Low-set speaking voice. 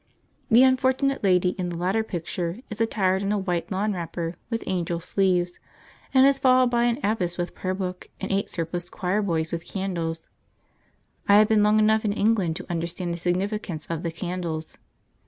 No: medium, 185 Hz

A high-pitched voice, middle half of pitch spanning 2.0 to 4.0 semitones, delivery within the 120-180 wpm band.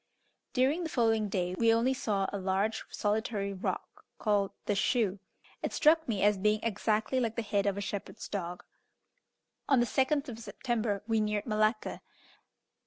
Yes: high, 215 Hz; average, 2.8 semitones; average, 165 wpm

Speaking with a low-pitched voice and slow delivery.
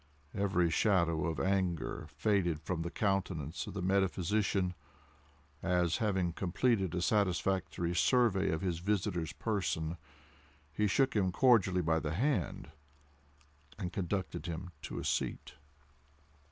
Yes: very low, 90 Hz; slow, 125 wpm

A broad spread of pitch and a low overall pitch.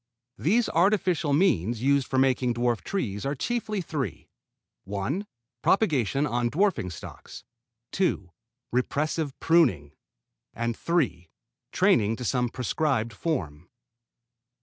Yes: wide, 6.5 semitones; low, 130 Hz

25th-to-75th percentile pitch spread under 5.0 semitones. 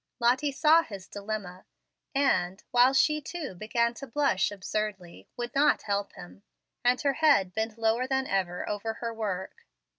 No: wide, 5.4 semitones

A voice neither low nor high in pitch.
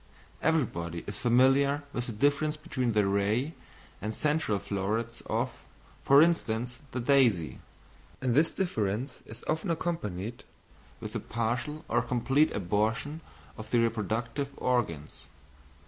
No: low, 120 Hz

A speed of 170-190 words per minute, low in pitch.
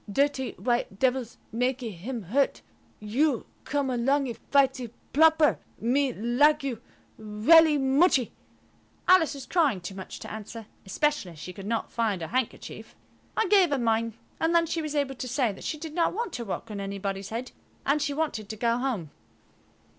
No: average, 175 wpm; very high, 255 Hz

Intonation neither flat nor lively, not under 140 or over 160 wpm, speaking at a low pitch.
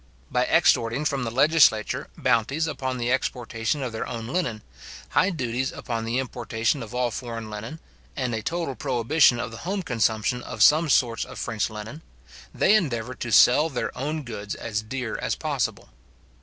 No: average, 3.8 semitones; average, 170 wpm; low, 125 Hz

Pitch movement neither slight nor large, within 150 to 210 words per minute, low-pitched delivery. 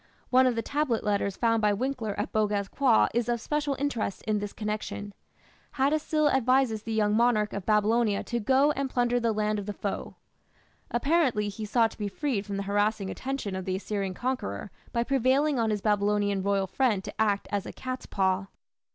No: average, 3.9 semitones; average, 195 wpm; high, 220 Hz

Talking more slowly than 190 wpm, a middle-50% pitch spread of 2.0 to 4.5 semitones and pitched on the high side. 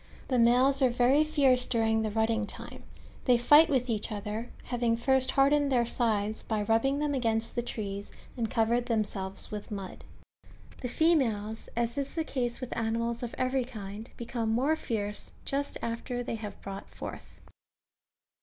Yes: average, 165 wpm; average, 2.8 semitones; high, 235 Hz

